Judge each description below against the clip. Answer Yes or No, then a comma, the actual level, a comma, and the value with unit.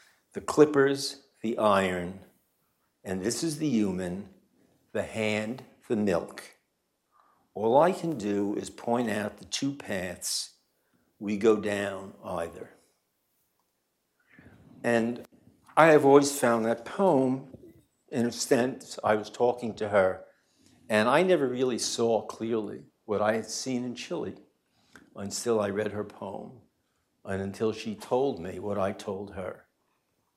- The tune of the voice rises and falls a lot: No, average, 4.2 semitones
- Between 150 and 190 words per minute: No, slow, 135 wpm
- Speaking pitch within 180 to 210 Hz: No, low, 115 Hz